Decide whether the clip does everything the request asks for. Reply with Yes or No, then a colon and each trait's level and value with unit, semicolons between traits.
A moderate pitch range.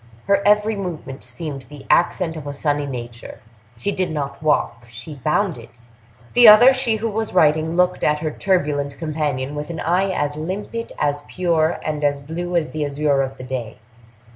Yes: average, 4.1 semitones